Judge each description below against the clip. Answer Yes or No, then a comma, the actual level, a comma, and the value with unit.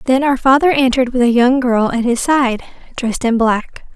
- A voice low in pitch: No, very high, 250 Hz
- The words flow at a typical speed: No, fast, 210 wpm